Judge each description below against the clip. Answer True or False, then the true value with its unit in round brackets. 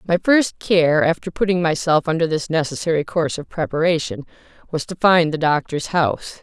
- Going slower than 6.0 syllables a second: True (5.4 syllables/s)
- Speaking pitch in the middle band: True (165 Hz)